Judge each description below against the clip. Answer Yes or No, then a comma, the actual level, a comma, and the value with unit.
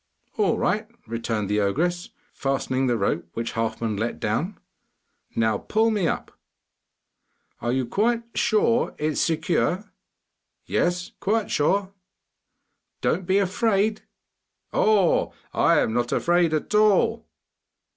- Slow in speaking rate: Yes, slow, 115 wpm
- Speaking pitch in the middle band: Yes, medium, 175 Hz